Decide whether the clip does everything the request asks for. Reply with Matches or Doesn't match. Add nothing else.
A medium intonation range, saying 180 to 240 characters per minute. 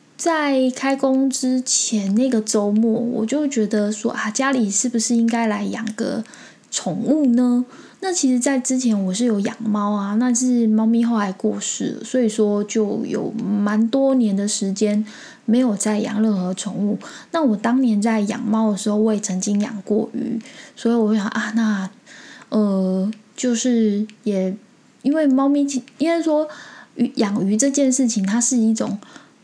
Matches